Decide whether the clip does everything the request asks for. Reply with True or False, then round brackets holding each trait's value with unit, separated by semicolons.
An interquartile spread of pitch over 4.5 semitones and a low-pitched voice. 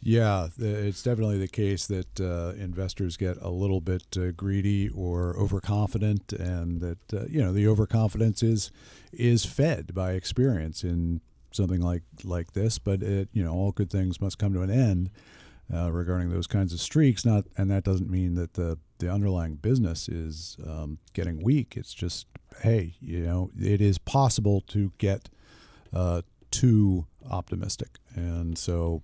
False (3.4 semitones; 95 Hz)